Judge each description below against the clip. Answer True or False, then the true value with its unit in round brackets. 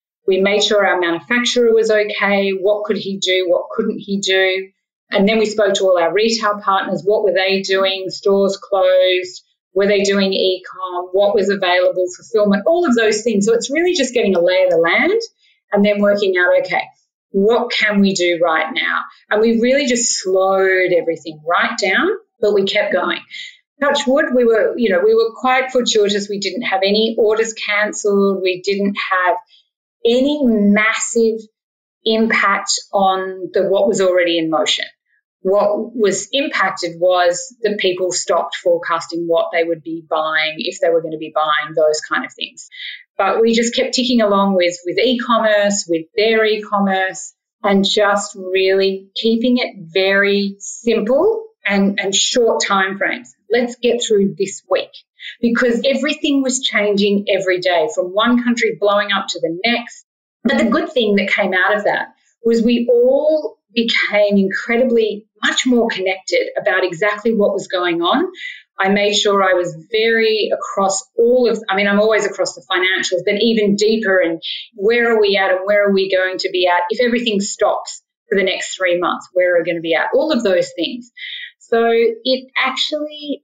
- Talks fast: False (180 wpm)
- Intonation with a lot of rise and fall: False (3.7 semitones)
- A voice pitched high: True (205 Hz)